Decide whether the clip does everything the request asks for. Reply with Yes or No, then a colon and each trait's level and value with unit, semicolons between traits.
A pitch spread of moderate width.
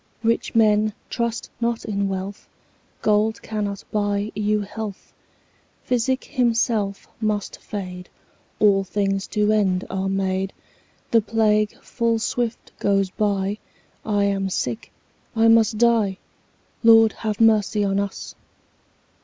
No: narrow, 2.2 semitones